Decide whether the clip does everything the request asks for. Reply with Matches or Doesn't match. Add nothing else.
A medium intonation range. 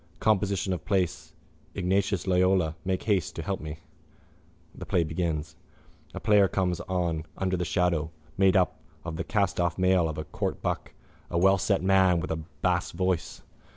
Doesn't match